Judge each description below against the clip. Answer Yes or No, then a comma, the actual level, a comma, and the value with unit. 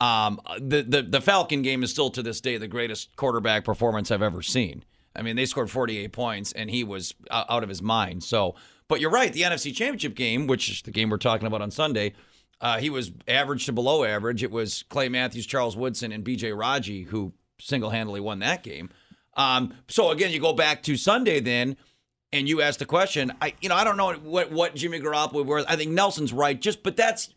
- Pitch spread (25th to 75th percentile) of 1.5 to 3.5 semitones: No, average, 5.1 semitones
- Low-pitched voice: Yes, low, 125 Hz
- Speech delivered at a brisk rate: Yes, fast, 230 wpm